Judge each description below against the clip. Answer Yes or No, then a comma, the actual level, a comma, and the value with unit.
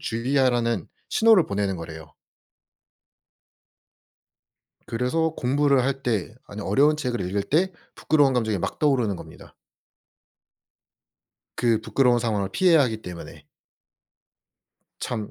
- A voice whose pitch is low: Yes, low, 120 Hz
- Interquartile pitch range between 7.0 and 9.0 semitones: No, wide, 5.4 semitones